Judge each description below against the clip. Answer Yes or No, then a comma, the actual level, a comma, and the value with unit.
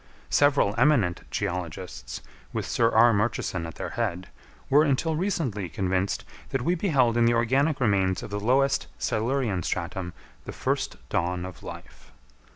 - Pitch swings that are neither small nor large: No, wide, 6.6 semitones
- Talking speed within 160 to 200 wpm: No, average, 150 wpm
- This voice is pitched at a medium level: No, low, 110 Hz